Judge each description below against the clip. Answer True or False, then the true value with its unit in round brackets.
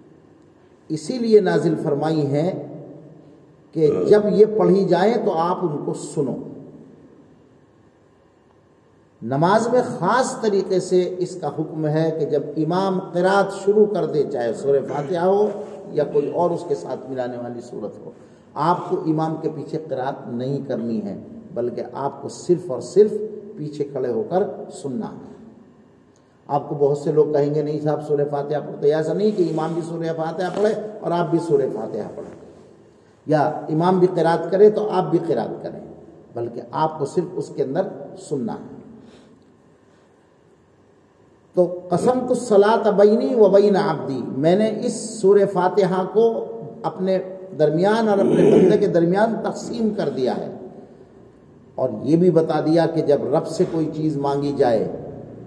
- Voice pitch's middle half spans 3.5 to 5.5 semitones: True (5.2 semitones)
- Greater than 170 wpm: False (160 wpm)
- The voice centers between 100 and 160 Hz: False (175 Hz)